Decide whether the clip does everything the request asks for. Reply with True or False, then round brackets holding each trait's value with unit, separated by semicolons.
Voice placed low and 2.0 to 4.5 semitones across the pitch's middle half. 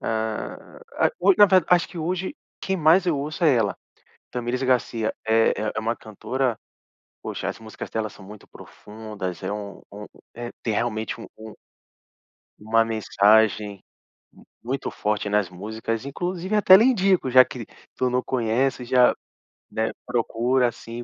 True (115 Hz; 3.9 semitones)